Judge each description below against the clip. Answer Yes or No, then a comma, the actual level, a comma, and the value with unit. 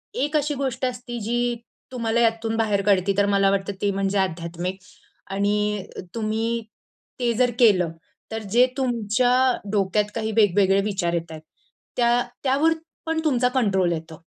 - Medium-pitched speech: No, high, 215 Hz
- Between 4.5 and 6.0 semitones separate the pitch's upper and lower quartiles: No, average, 3.7 semitones